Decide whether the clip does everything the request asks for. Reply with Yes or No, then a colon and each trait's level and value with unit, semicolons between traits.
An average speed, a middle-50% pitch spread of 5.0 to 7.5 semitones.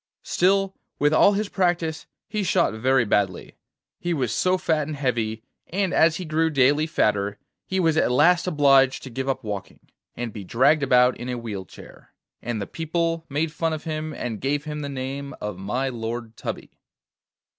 Yes: average, 185 wpm; wide, 5.4 semitones